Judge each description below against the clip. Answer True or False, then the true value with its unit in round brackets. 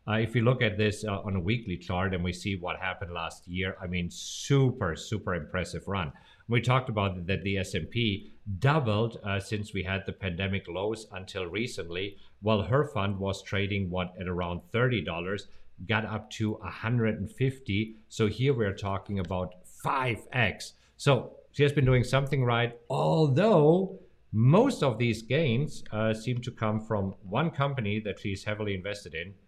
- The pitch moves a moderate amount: True (3.8 semitones)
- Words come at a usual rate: True (170 wpm)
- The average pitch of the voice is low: True (105 Hz)